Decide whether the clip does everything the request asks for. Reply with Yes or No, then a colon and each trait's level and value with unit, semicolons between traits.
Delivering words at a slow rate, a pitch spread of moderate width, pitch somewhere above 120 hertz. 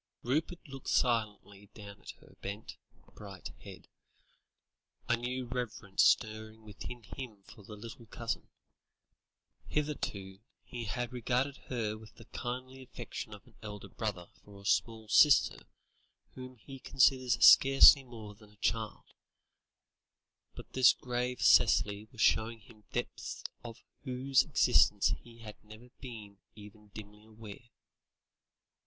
No: slow, 130 wpm; average, 3.1 semitones; low, 115 Hz